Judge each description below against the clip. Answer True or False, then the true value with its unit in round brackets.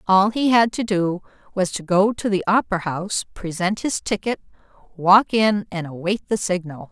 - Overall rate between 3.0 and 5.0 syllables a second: True (4.8 syllables/s)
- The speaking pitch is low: False (195 Hz)